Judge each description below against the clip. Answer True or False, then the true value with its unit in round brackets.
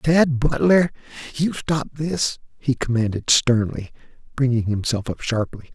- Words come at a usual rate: False (125 wpm)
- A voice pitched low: True (130 Hz)